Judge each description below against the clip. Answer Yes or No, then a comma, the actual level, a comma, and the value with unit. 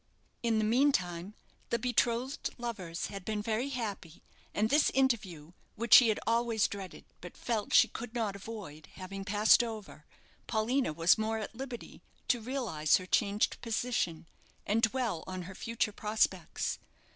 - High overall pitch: Yes, high, 220 Hz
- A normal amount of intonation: Yes, average, 3.6 semitones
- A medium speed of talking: Yes, average, 150 wpm